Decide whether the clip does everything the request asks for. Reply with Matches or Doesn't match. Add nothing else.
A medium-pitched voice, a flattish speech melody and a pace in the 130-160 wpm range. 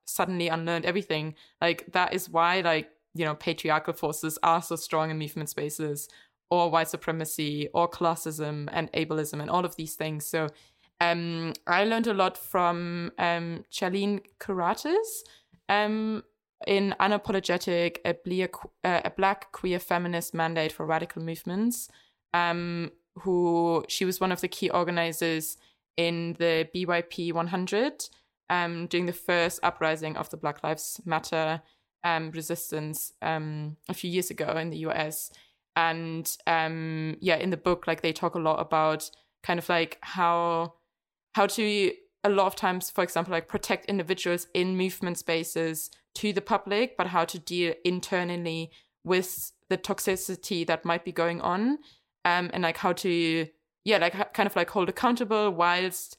Matches